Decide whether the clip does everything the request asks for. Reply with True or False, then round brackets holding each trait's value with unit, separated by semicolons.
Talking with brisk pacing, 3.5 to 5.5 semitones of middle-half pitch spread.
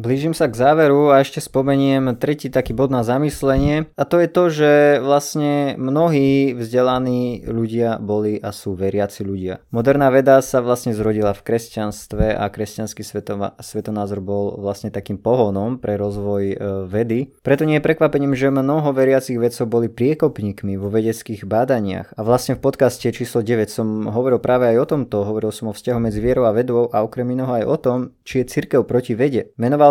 True (180 wpm; 4.2 semitones)